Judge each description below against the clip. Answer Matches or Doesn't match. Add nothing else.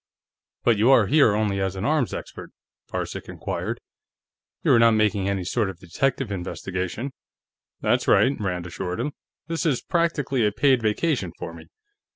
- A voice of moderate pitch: Doesn't match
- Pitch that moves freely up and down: Matches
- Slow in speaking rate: Doesn't match